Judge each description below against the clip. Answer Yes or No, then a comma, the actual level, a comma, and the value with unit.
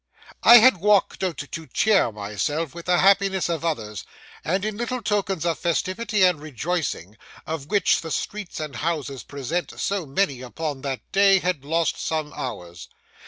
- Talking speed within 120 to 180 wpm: Yes, average, 165 wpm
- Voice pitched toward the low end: No, medium, 165 Hz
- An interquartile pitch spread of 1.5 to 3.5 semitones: No, wide, 5.5 semitones